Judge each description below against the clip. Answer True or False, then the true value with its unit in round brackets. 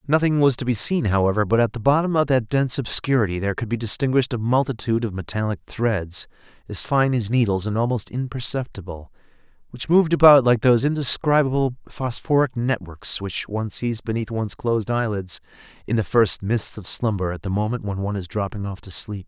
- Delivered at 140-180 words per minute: False (190 wpm)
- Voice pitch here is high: False (115 Hz)